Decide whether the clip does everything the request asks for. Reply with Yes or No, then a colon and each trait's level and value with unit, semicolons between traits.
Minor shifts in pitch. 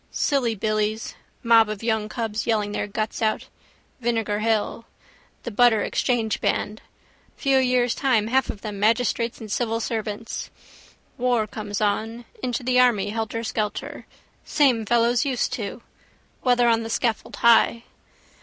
Yes: narrow, 2.1 semitones